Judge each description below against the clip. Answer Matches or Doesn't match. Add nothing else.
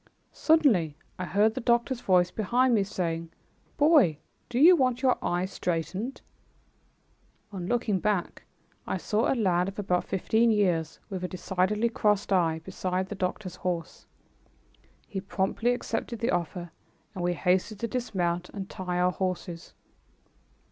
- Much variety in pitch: Doesn't match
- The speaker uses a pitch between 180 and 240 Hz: Matches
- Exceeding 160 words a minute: Doesn't match